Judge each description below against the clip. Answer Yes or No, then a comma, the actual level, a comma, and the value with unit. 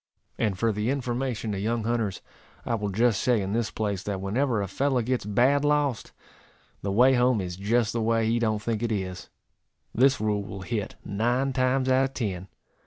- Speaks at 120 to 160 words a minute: No, average, 195 wpm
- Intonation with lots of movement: No, average, 3.7 semitones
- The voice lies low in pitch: Yes, low, 115 Hz